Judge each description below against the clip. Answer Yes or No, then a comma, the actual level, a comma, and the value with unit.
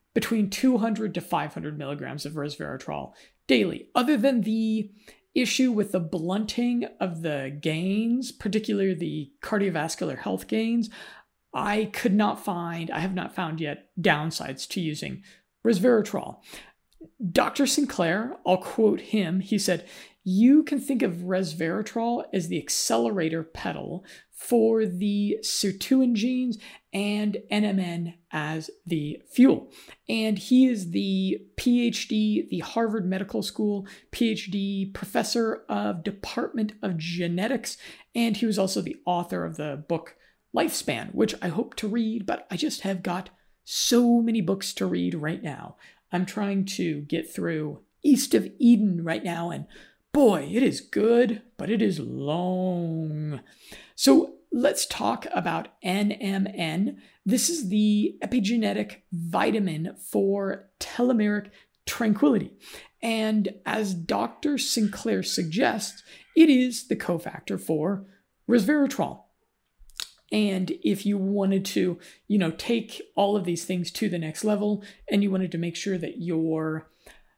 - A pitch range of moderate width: Yes, average, 4.4 semitones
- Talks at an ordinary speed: No, slow, 130 wpm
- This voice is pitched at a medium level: No, high, 200 Hz